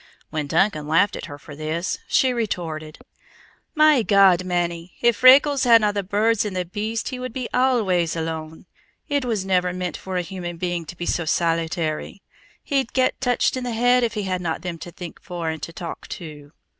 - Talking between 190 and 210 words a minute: Yes, average, 195 wpm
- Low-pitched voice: No, medium, 185 Hz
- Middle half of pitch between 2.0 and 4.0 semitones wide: No, wide, 5.5 semitones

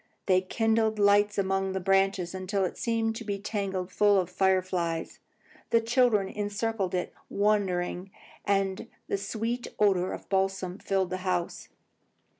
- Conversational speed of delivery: Yes, average, 150 wpm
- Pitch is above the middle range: Yes, high, 195 Hz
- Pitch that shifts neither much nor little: No, narrow, 2.0 semitones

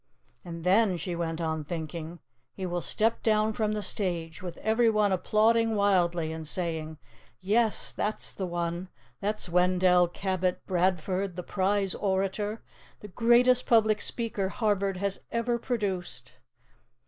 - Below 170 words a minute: Yes, slow, 135 wpm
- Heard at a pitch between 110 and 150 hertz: No, high, 190 Hz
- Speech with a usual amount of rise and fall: Yes, average, 3.5 semitones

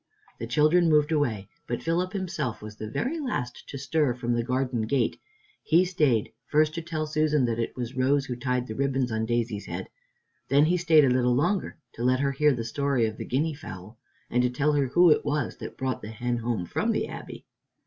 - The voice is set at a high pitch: No, low, 130 Hz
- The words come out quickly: Yes, fast, 220 wpm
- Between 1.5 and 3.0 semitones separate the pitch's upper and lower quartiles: No, average, 4.2 semitones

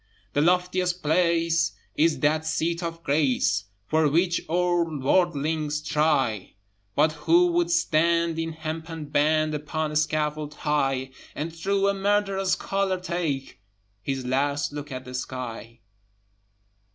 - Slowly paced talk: Yes, slow, 125 wpm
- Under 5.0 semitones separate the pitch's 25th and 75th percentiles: Yes, average, 2.8 semitones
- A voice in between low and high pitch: Yes, medium, 155 Hz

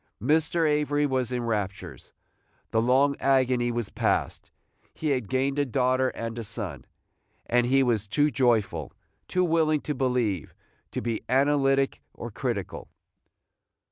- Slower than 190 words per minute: Yes, average, 140 wpm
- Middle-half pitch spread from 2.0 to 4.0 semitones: Yes, average, 3.5 semitones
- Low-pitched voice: Yes, low, 130 Hz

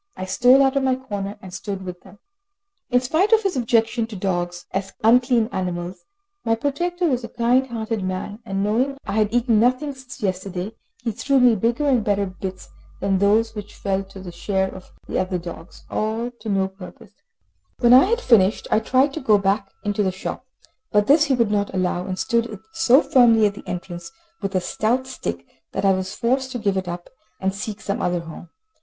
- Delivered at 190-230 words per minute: Yes, average, 200 wpm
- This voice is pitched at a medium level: No, high, 215 Hz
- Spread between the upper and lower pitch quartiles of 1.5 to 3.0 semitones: No, average, 4.6 semitones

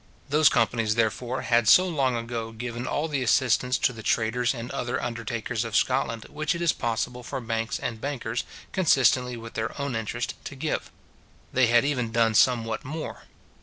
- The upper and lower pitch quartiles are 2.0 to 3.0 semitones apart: Yes, narrow, 2.6 semitones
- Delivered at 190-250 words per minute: No, average, 175 wpm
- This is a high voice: No, low, 120 Hz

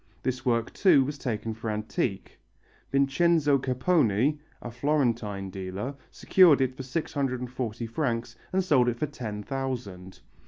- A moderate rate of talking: No, slow, 130 wpm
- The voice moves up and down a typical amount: Yes, average, 3.9 semitones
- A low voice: Yes, low, 125 Hz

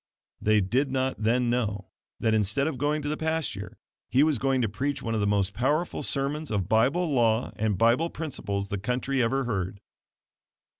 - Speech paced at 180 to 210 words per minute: Yes, average, 185 wpm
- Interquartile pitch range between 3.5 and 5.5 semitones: Yes, average, 4.9 semitones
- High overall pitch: No, low, 125 Hz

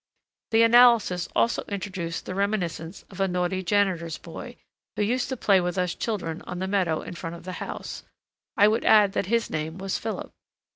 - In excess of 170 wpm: Yes, average, 190 wpm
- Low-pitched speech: No, high, 190 Hz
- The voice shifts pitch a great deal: No, average, 3.2 semitones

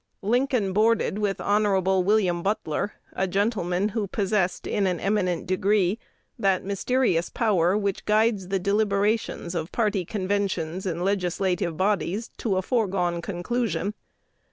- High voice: Yes, high, 195 Hz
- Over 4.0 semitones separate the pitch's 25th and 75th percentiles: No, average, 2.7 semitones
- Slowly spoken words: Yes, slow, 130 wpm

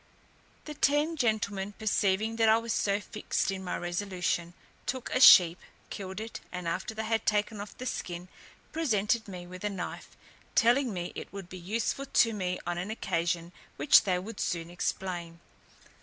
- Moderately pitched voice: No, high, 200 Hz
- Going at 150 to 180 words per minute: Yes, average, 170 wpm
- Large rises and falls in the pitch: No, average, 3.9 semitones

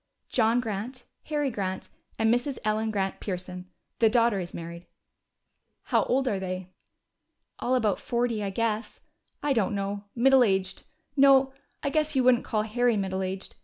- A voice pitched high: Yes, high, 220 Hz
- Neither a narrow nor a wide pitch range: Yes, average, 4.4 semitones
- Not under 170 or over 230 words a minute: No, average, 160 wpm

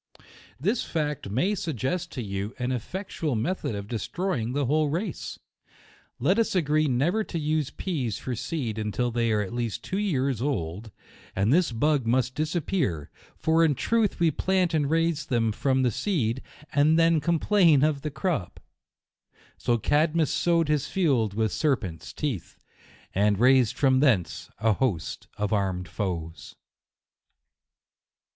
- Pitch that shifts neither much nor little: No, wide, 6.4 semitones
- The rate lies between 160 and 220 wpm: No, average, 150 wpm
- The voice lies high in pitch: No, low, 135 Hz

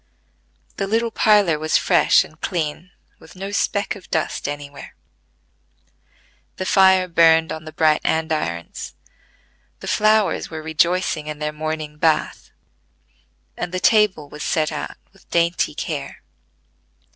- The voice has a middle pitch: Yes, medium, 160 Hz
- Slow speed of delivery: Yes, slow, 130 wpm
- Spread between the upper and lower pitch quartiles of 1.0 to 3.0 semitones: No, average, 3.5 semitones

